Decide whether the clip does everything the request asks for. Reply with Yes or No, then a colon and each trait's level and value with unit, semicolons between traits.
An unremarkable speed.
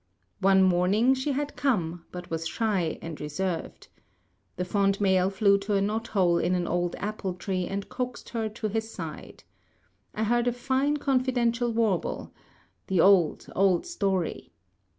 Yes: average, 155 wpm